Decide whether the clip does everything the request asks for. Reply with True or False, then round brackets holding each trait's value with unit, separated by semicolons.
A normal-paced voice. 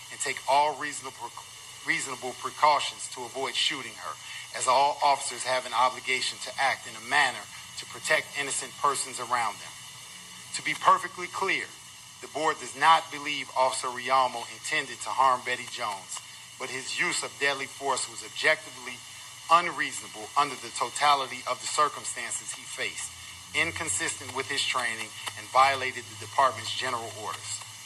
True (150 wpm)